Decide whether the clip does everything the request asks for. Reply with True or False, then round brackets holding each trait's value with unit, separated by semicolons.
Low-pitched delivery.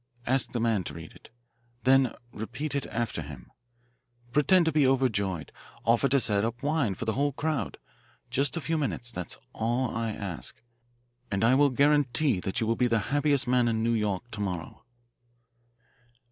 True (120 Hz)